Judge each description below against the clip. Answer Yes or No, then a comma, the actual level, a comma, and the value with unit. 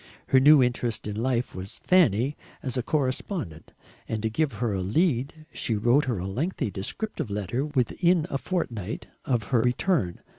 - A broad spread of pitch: Yes, wide, 5.9 semitones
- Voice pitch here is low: Yes, low, 125 Hz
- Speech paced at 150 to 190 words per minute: Yes, average, 170 wpm